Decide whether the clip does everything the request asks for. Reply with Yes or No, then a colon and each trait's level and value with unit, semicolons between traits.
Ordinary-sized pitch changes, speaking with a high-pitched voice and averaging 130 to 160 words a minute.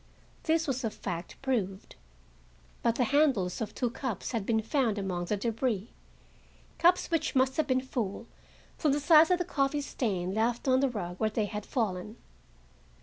No: average, 4.9 semitones; high, 235 Hz; average, 170 wpm